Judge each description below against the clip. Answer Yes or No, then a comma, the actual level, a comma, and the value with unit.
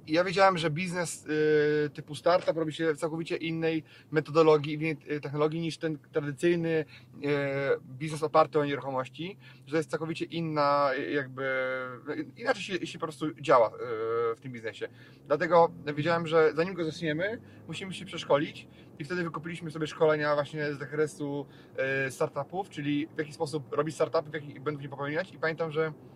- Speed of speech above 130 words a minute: Yes, average, 155 wpm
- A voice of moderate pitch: Yes, medium, 155 Hz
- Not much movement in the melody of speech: Yes, narrow, 2.1 semitones